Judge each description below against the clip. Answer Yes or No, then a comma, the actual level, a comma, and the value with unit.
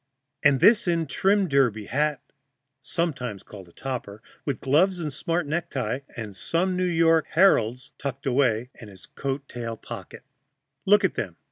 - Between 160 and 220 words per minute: No, average, 150 wpm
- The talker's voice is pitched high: No, medium, 140 Hz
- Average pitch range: No, wide, 6.1 semitones